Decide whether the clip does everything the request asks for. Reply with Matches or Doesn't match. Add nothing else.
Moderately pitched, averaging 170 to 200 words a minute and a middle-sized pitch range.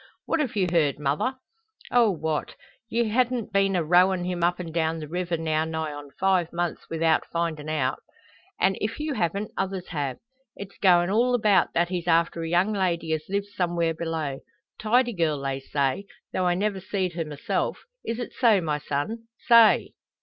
Matches